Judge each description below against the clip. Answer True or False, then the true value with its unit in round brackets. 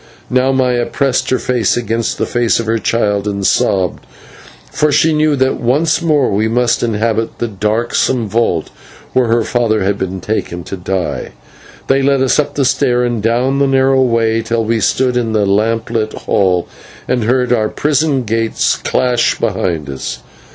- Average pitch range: True (3.3 semitones)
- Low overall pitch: True (115 Hz)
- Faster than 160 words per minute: True (175 wpm)